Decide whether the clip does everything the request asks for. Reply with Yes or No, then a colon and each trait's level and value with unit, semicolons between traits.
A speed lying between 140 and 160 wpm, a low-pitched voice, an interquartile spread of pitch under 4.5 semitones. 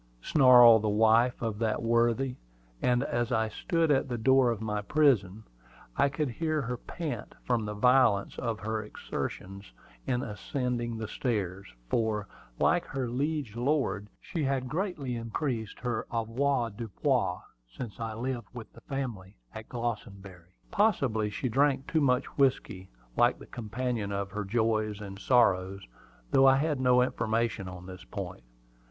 Yes: average, 150 wpm; low, 120 Hz; average, 3.9 semitones